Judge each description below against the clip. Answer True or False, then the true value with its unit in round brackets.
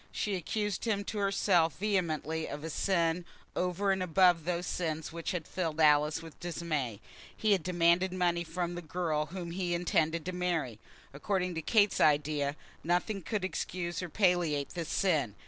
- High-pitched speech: False (175 Hz)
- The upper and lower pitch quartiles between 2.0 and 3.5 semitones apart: True (2.6 semitones)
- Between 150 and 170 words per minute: True (165 wpm)